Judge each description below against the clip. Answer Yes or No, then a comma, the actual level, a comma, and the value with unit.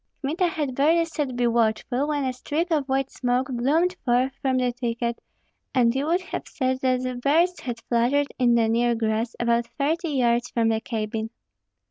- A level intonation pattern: No, average, 3.5 semitones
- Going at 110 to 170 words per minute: No, average, 180 wpm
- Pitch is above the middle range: Yes, very high, 255 Hz